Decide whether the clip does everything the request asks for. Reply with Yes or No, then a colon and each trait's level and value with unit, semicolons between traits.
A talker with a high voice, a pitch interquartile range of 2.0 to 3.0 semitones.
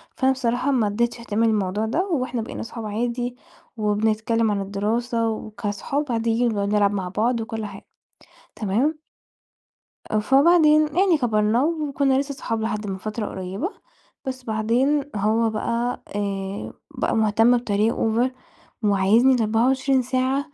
No: high, 230 Hz; average, 3.5 semitones